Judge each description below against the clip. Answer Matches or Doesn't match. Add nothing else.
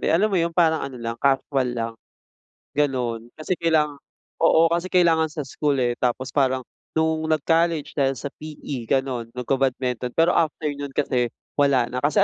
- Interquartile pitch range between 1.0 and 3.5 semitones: Doesn't match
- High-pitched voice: Doesn't match